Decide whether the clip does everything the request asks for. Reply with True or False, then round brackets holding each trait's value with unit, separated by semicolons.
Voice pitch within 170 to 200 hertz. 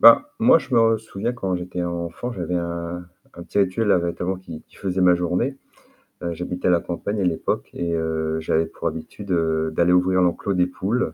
False (90 Hz)